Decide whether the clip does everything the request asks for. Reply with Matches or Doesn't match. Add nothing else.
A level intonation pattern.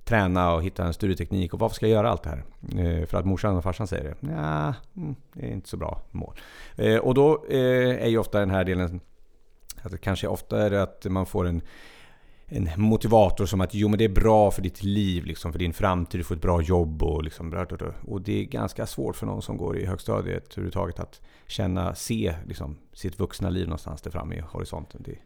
Doesn't match